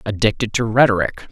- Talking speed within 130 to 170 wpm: Yes, slow, 135 wpm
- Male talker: Yes, male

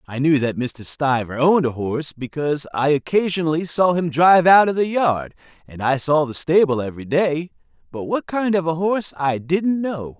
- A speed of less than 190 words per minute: No, average, 195 wpm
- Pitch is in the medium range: Yes, medium, 155 Hz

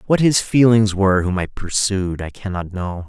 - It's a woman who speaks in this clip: No, male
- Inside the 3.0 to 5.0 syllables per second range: Yes, 4.8 syllables/s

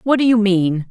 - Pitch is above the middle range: Yes, high, 205 Hz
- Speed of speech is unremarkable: No, fast, 265 wpm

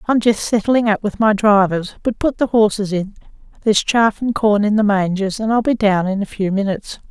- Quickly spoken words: Yes, fast, 230 wpm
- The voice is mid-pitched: No, high, 210 Hz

